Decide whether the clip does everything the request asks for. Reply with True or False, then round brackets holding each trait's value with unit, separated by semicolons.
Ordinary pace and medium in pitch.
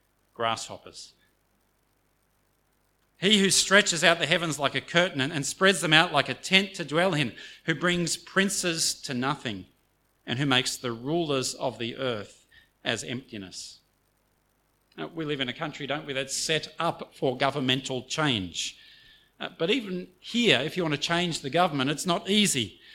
True (160 wpm; 145 Hz)